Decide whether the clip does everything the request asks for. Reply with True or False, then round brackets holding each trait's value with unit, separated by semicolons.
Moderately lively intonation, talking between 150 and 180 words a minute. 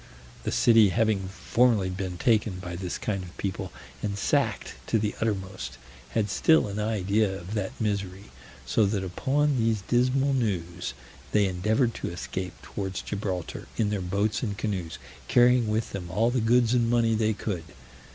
True (3.2 semitones; 165 wpm)